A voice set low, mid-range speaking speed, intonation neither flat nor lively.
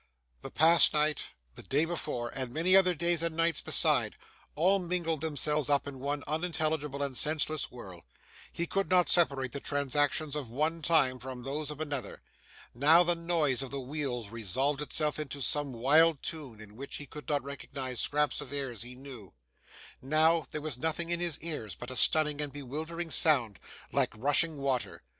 No: medium, 145 Hz; average, 175 wpm; average, 3.3 semitones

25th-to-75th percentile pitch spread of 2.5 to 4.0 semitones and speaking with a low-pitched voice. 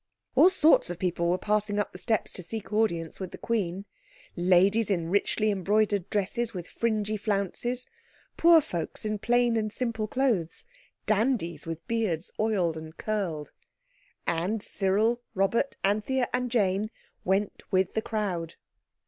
No: average, 3.7 semitones; high, 205 Hz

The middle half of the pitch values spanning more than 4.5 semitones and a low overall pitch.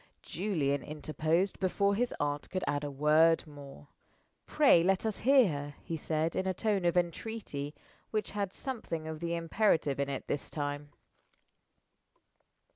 No: average, 5.1 semitones; medium, 165 Hz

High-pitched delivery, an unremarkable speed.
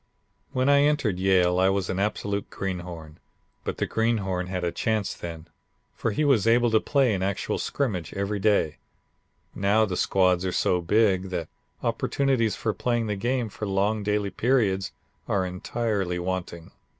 No: low, 100 Hz; average, 160 wpm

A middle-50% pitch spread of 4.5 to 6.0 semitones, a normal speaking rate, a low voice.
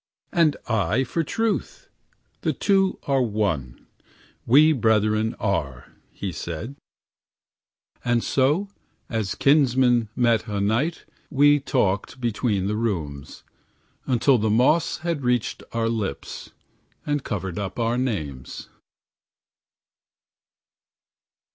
No: average, 5.1 semitones; slow, 105 wpm; low, 115 Hz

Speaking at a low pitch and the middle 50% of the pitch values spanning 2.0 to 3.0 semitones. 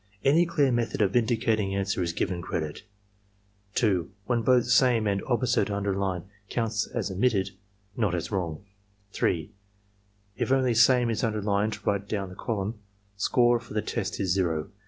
No: low, 105 Hz; average, 3.6 semitones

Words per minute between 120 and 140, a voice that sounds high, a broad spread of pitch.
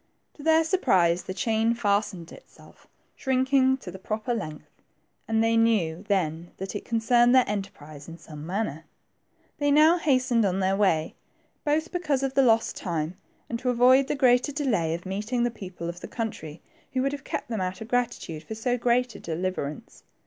No: average, 185 wpm; high, 225 Hz; wide, 6.0 semitones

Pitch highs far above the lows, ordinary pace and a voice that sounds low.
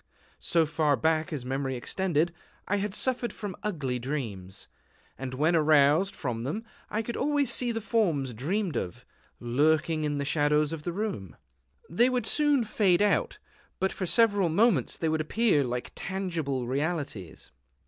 No: wide, 6.6 semitones; average, 160 wpm; medium, 160 Hz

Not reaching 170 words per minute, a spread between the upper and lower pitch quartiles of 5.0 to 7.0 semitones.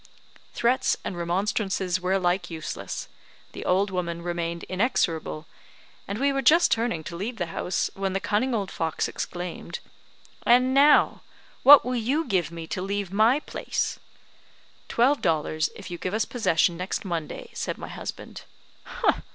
Yes: average, 150 wpm; wide, 5.4 semitones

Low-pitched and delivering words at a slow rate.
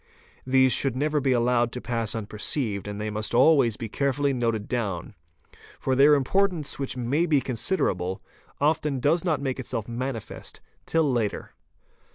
No: low, 130 Hz; average, 160 wpm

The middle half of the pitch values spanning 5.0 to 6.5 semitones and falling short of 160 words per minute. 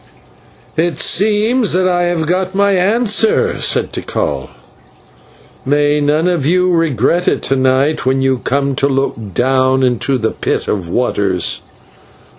Yes: wide, 5.6 semitones; average, 140 wpm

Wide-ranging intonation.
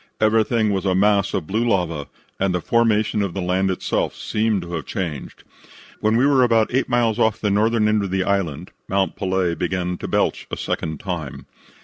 No: average, 3.3 semitones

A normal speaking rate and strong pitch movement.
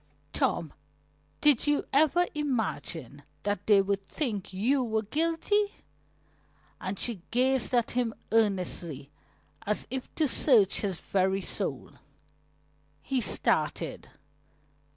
No: slow, 105 wpm; wide, 5.8 semitones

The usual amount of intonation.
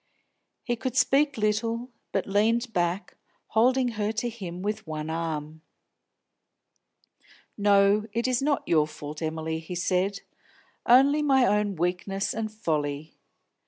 No: wide, 5.8 semitones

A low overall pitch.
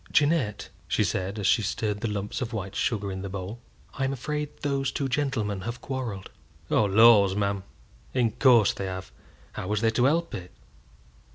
Yes: low, 110 Hz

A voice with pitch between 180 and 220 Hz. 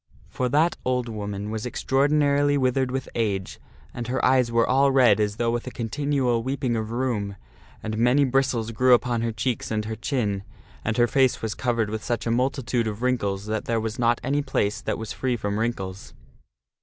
No: low, 120 Hz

